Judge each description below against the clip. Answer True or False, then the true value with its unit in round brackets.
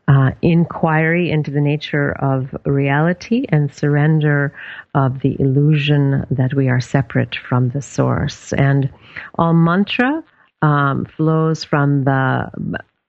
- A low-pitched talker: False (145 Hz)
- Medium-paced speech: False (120 wpm)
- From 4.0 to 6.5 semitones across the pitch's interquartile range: False (2.5 semitones)